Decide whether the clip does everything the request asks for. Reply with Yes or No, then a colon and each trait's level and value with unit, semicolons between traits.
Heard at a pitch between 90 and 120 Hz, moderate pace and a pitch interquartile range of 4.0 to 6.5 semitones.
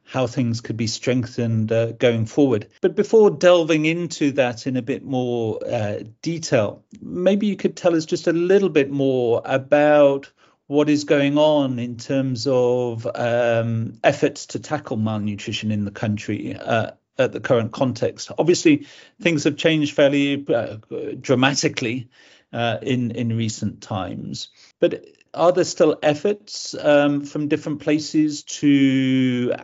No: low, 135 Hz; average, 145 wpm; average, 4.6 semitones